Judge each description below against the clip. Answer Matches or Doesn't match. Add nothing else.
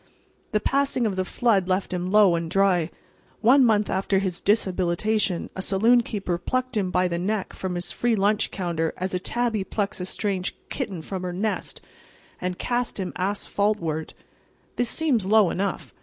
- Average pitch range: Matches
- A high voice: Matches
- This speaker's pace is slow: Doesn't match